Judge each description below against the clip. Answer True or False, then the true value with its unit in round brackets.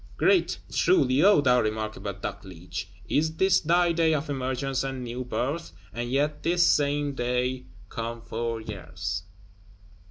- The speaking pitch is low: True (130 Hz)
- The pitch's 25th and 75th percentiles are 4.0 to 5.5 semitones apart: True (4.9 semitones)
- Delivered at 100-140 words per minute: True (135 wpm)